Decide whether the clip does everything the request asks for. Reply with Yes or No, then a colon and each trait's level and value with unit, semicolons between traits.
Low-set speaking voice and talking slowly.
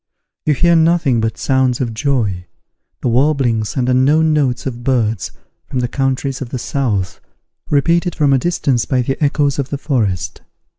No: low, 130 Hz; average, 165 wpm